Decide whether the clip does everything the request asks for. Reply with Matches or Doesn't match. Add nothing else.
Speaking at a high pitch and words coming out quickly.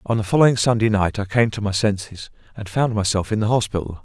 Doesn't match